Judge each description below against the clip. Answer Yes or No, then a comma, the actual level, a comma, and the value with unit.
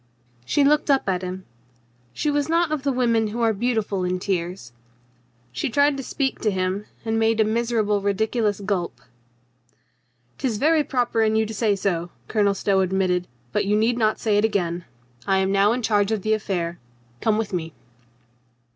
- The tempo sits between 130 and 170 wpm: No, average, 185 wpm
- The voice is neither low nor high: No, high, 215 Hz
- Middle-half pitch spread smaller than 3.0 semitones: No, average, 3.5 semitones